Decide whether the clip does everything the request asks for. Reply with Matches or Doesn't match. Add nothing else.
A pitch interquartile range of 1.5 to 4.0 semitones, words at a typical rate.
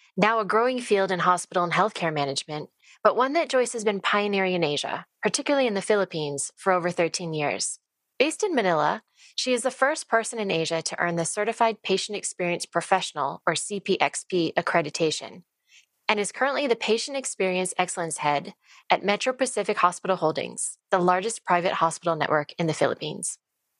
Doesn't match